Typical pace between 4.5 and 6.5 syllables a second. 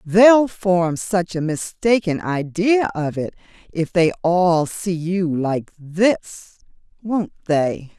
No: 3.2 syllables/s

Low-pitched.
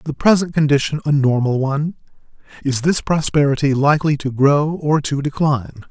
No: medium, 145 Hz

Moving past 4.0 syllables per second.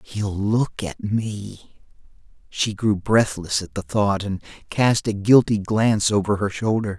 No: 3.9 syllables/s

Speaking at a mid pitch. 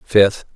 No: low, 100 Hz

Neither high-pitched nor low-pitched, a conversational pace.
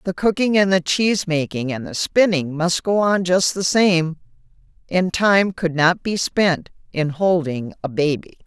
Yes: medium, 175 Hz; average, 175 wpm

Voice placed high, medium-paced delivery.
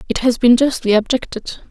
Yes: high, 240 Hz; average, 175 wpm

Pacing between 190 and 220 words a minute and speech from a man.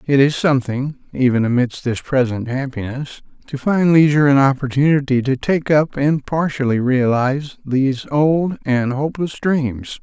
No: average, 145 wpm; male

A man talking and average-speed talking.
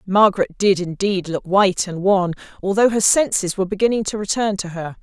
No: female; average, 190 wpm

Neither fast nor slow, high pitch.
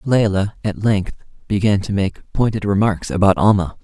No: average, 155 wpm; low, 100 Hz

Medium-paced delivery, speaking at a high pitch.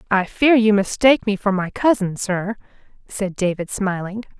Yes: average, 165 wpm; high, 205 Hz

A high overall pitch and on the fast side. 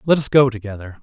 No: low, 120 Hz; fast, 235 wpm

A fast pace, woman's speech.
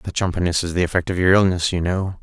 No: fast, 270 wpm; male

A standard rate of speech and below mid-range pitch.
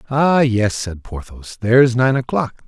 Yes: average, 180 wpm; low, 120 Hz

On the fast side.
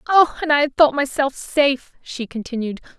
No: average, 160 wpm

